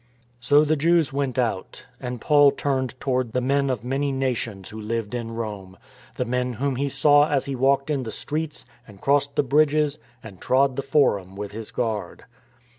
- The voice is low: Yes, low, 130 Hz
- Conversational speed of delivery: Yes, average, 190 wpm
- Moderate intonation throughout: Yes, average, 3.7 semitones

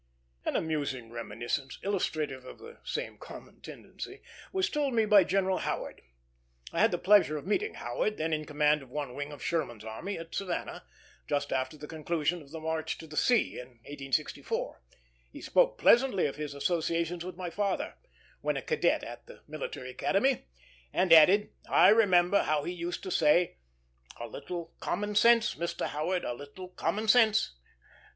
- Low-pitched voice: No, medium, 170 Hz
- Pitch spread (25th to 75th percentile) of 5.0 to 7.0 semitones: Yes, wide, 5.6 semitones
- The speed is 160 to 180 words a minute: Yes, average, 170 wpm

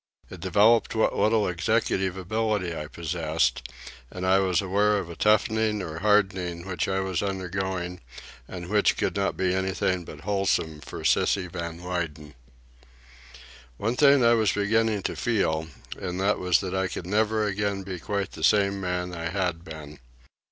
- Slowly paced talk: No, average, 165 wpm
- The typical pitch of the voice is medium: No, very low, 95 Hz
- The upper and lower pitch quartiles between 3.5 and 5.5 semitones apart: No, average, 2.9 semitones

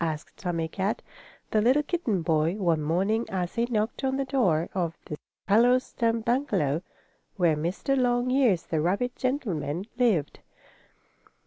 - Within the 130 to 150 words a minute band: Yes, average, 140 wpm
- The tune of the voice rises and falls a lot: Yes, wide, 6.8 semitones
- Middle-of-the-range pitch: No, high, 200 Hz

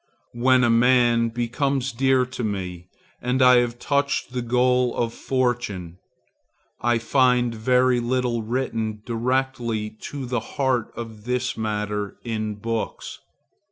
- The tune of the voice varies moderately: No, narrow, 2.1 semitones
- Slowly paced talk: Yes, slow, 125 wpm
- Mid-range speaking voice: No, low, 120 Hz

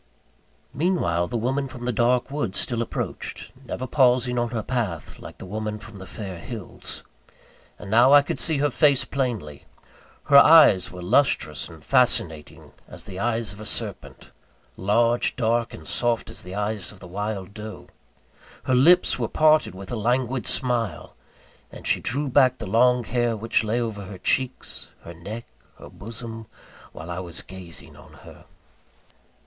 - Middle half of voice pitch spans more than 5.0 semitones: No, average, 4.4 semitones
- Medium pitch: No, low, 115 Hz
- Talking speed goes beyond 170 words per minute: No, average, 165 wpm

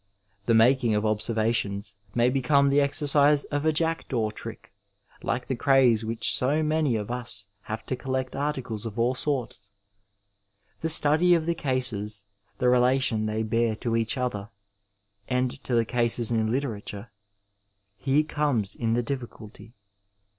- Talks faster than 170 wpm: No, average, 150 wpm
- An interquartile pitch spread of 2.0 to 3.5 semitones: No, average, 4.0 semitones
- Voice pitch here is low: Yes, low, 120 Hz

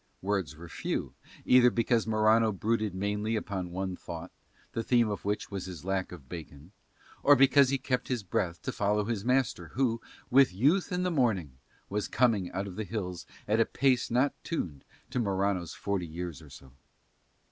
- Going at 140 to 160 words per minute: No, average, 180 wpm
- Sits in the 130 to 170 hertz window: No, low, 105 Hz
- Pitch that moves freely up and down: No, average, 4.9 semitones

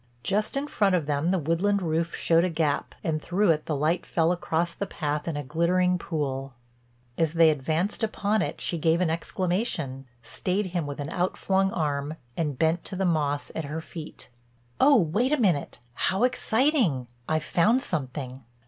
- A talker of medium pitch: Yes, medium, 165 Hz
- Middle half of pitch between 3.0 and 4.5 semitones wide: Yes, average, 4.1 semitones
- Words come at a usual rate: Yes, average, 175 wpm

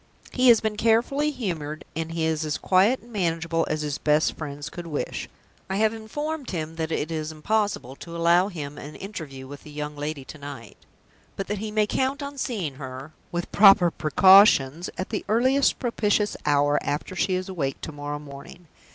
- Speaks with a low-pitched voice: No, medium, 170 Hz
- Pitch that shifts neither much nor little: No, wide, 6.0 semitones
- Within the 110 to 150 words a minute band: No, average, 195 wpm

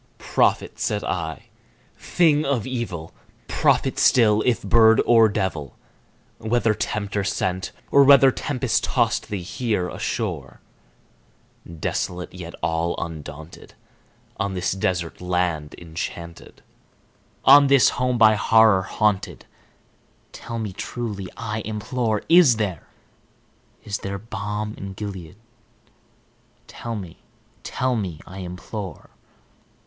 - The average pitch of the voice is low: Yes, low, 105 Hz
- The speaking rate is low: Yes, slow, 110 wpm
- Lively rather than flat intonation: No, average, 4.4 semitones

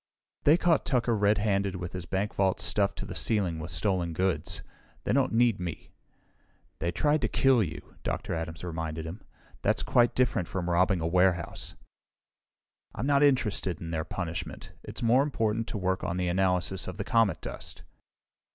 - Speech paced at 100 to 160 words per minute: No, average, 170 wpm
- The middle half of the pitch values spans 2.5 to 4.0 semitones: No, average, 4.8 semitones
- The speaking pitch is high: No, very low, 95 Hz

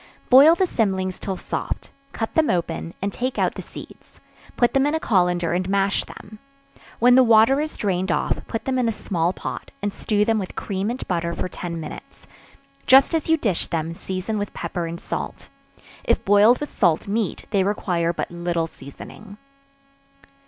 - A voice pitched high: Yes, high, 200 Hz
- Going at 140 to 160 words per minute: No, average, 185 wpm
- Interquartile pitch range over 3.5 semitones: Yes, average, 5.0 semitones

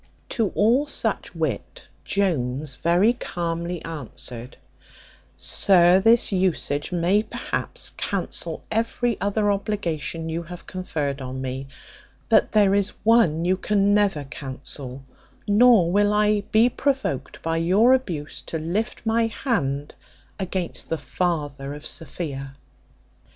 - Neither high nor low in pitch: Yes, medium, 180 Hz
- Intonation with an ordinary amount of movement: No, wide, 5.9 semitones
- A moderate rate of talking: No, slow, 120 wpm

